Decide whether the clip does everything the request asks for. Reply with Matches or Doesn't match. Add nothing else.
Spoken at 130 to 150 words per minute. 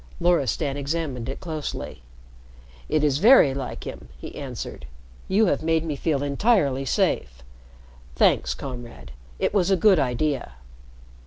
Matches